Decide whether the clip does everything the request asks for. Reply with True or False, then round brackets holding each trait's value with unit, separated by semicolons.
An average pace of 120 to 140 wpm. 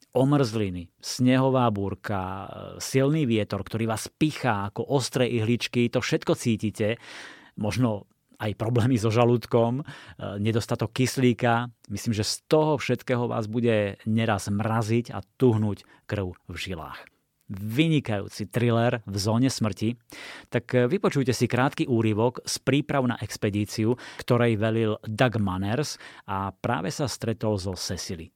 True (125 wpm)